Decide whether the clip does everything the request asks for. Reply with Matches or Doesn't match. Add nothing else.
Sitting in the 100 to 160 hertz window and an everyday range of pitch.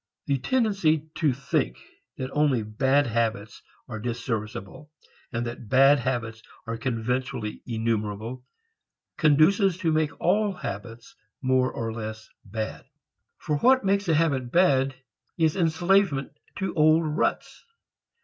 Doesn't match